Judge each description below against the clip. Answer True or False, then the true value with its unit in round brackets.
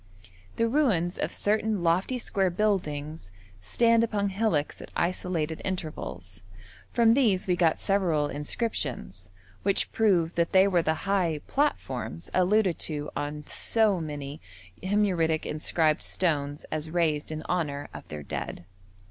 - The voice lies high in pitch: False (170 Hz)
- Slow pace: True (130 wpm)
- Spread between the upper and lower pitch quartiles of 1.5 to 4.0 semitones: False (5.1 semitones)